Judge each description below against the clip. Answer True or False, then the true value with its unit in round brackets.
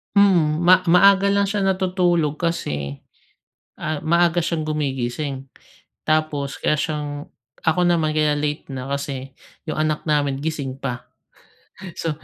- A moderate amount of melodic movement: True (3.5 semitones)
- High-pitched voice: False (155 Hz)